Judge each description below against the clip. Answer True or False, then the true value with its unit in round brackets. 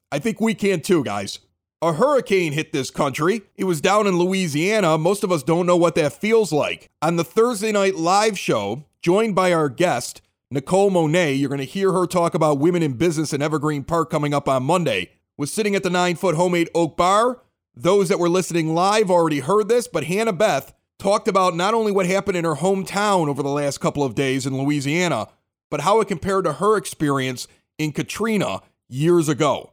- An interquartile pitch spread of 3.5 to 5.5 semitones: True (4.6 semitones)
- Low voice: False (175 Hz)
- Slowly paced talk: False (205 wpm)